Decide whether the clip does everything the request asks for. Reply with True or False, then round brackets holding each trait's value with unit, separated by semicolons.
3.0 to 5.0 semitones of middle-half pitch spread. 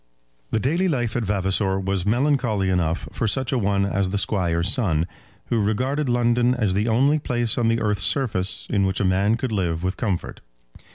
True (4.1 semitones)